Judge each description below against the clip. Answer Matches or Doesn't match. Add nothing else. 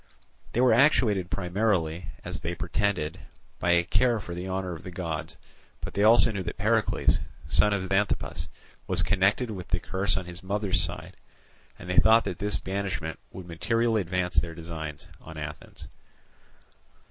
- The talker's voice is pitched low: Matches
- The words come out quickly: Doesn't match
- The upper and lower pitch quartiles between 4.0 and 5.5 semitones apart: Doesn't match